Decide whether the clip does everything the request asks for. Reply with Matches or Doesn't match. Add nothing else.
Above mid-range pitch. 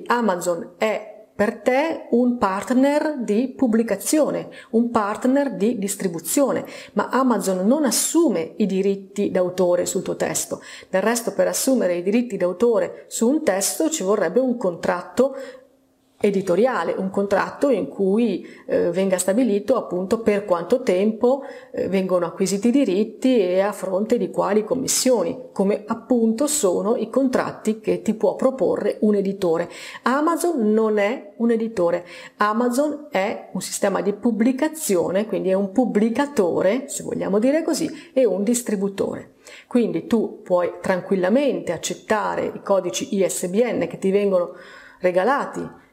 Matches